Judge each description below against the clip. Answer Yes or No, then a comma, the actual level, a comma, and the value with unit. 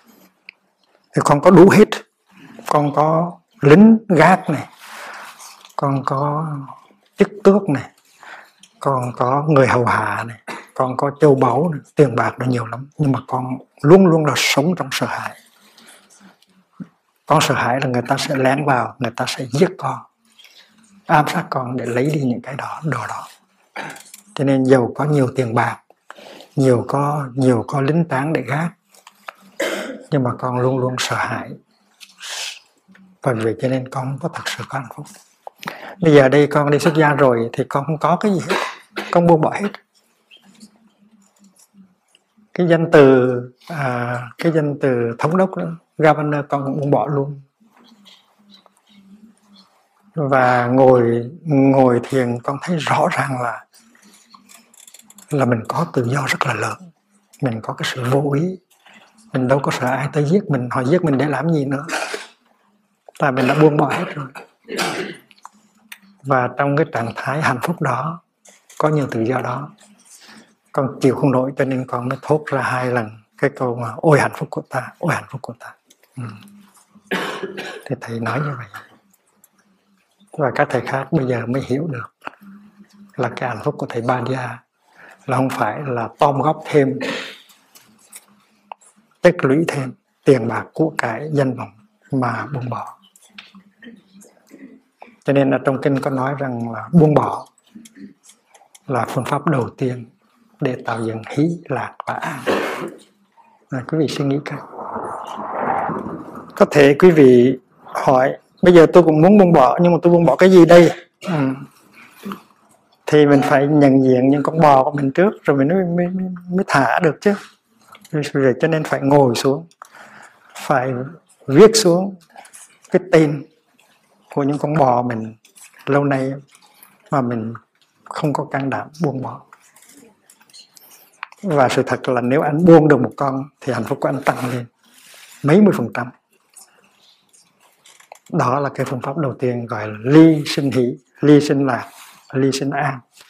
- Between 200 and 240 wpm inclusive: No, slow, 165 wpm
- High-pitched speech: No, medium, 145 Hz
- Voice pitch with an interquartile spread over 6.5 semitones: No, average, 5.3 semitones